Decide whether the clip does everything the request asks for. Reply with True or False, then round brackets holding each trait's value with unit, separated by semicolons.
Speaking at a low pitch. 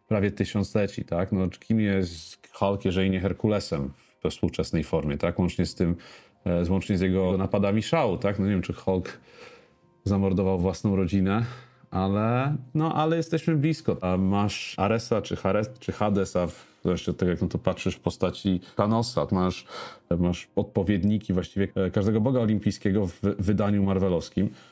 True (95 Hz)